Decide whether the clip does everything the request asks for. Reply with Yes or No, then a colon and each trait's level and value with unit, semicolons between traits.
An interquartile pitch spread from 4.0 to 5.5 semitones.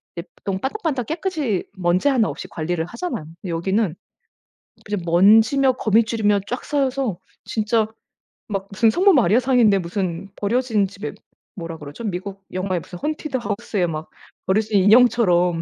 Yes: average, 5.2 semitones